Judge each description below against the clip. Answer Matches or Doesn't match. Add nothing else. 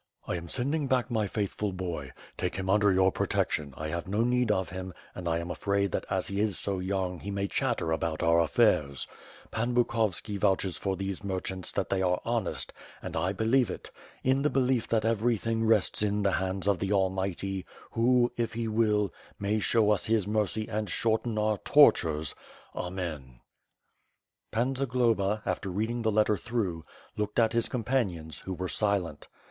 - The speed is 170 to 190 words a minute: Matches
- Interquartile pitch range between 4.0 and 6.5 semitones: Doesn't match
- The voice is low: Matches